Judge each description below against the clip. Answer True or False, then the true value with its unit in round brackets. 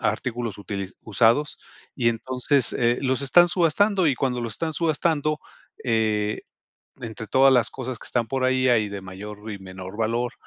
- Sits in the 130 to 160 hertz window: False (120 Hz)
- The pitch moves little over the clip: False (4.1 semitones)